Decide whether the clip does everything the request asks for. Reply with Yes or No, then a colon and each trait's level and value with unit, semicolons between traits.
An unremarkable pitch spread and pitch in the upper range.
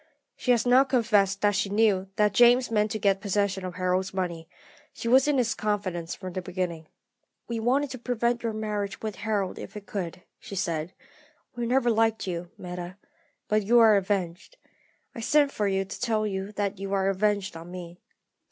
Yes: average, 3.4 semitones; high, 205 Hz